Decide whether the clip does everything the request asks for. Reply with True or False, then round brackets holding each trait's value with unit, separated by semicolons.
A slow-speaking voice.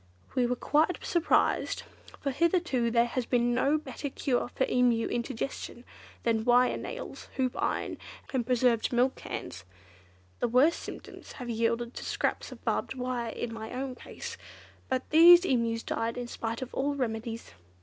False (160 wpm)